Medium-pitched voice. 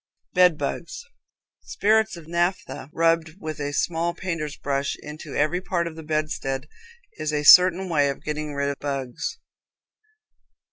Yes: medium, 155 Hz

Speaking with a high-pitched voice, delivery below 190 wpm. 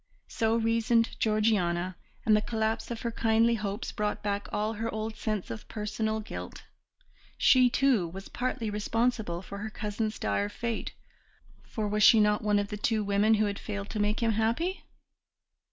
Yes: high, 215 Hz; average, 170 wpm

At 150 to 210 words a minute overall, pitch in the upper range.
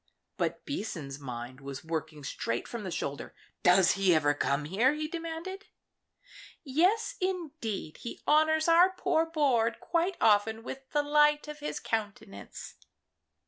No: average, 140 wpm; high, 240 Hz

